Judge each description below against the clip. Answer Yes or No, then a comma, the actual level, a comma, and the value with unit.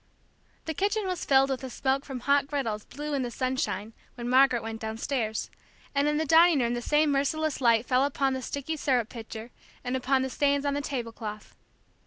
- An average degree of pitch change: Yes, average, 3.0 semitones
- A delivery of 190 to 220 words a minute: Yes, average, 200 wpm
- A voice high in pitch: Yes, very high, 265 Hz